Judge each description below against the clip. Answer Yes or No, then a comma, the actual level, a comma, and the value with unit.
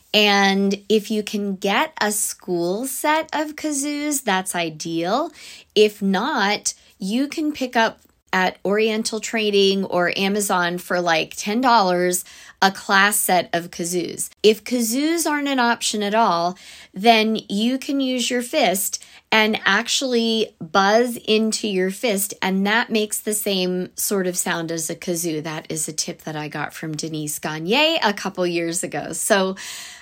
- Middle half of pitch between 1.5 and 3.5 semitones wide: No, average, 4.5 semitones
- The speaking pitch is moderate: No, high, 205 Hz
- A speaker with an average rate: Yes, average, 150 wpm